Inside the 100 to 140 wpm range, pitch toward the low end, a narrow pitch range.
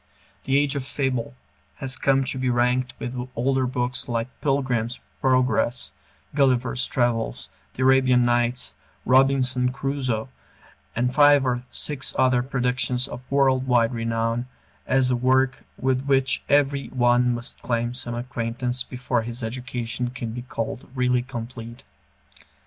Yes: slow, 135 wpm; low, 125 Hz; narrow, 1.6 semitones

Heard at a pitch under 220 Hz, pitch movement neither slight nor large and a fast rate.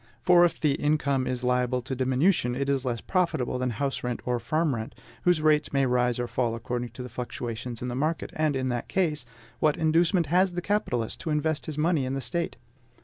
Yes: low, 135 Hz; average, 4.2 semitones; fast, 215 wpm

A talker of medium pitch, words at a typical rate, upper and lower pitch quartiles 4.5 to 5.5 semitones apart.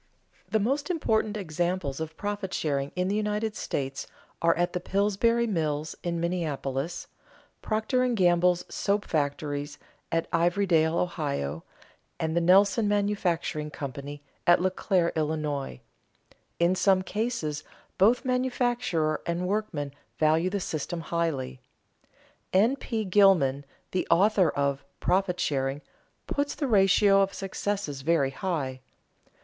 No: medium, 175 Hz; slow, 120 wpm; average, 5.1 semitones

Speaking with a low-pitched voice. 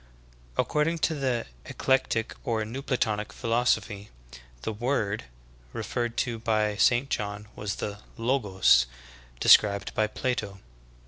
Yes: low, 110 Hz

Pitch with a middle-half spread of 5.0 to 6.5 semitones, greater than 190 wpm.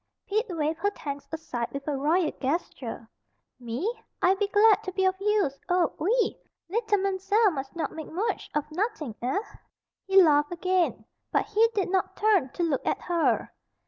No: wide, 5.4 semitones; average, 175 wpm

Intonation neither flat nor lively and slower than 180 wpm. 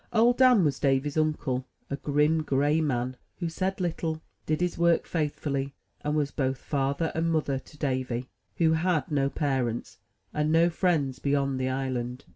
Yes: average, 3.3 semitones; average, 170 wpm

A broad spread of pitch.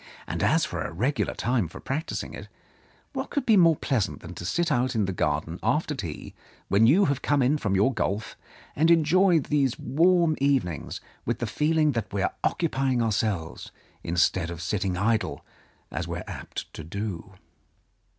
Yes: wide, 7.7 semitones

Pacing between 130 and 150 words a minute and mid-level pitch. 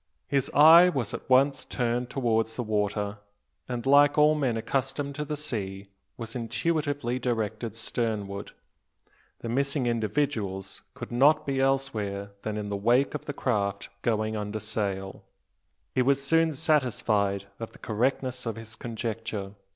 No: average, 145 wpm; low, 120 Hz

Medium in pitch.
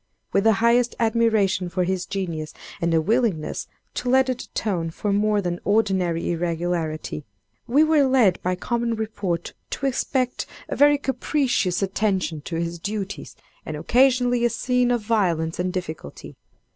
No: high, 200 Hz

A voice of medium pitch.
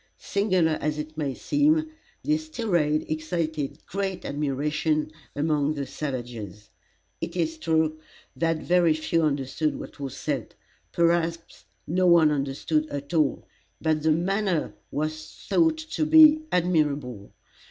Yes: medium, 155 Hz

